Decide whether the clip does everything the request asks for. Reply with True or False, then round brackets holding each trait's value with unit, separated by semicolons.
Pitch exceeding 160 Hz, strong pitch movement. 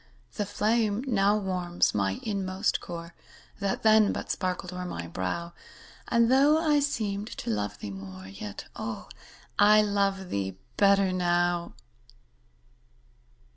False (190 Hz; 3.7 semitones)